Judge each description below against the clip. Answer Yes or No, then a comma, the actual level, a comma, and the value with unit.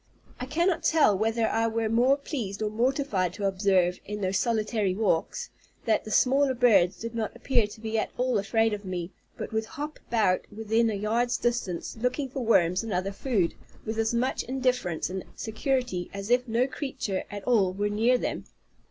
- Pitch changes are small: No, average, 3.9 semitones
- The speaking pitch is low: No, high, 220 Hz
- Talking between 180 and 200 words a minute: Yes, average, 185 wpm